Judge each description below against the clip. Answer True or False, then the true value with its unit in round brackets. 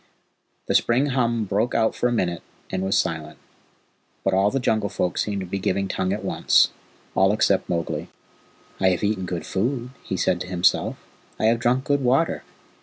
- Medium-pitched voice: False (100 Hz)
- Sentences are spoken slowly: False (185 wpm)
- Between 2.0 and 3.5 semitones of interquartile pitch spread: False (4.1 semitones)